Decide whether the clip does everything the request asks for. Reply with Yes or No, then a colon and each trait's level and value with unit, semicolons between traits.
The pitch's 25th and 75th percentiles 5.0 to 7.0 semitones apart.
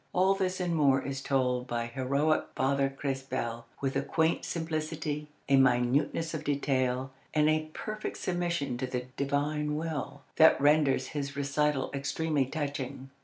No: average, 2.7 semitones